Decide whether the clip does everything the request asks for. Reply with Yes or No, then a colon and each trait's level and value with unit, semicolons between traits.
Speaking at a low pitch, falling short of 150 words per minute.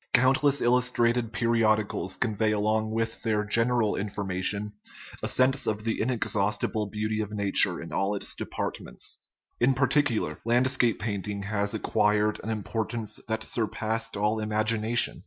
Yes: low, 110 Hz; average, 140 wpm